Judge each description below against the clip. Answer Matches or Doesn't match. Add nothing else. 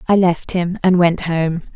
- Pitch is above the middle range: Doesn't match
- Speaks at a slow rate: Doesn't match